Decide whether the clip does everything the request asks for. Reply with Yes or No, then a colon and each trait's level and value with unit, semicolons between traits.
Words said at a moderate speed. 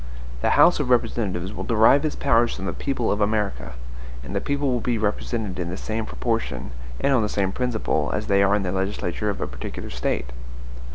No: fast, 210 wpm